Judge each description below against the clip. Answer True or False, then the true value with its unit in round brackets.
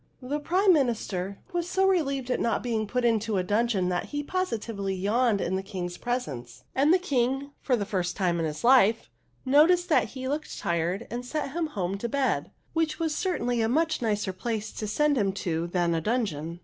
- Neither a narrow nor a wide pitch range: False (6.8 semitones)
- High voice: True (235 Hz)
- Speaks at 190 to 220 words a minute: True (205 wpm)